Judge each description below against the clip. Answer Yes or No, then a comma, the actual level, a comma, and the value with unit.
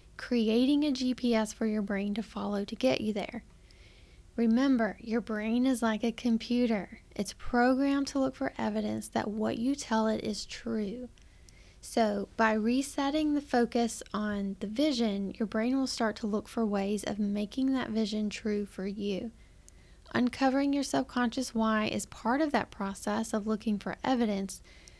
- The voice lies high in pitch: Yes, high, 225 Hz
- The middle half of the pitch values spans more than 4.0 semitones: No, average, 3.1 semitones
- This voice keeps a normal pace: Yes, average, 165 wpm